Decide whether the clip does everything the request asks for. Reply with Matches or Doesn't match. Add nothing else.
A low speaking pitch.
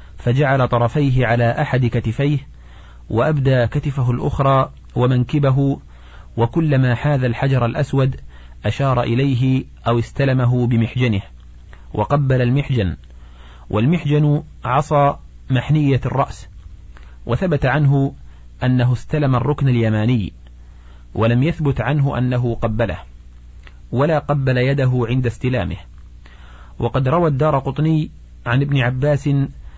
Matches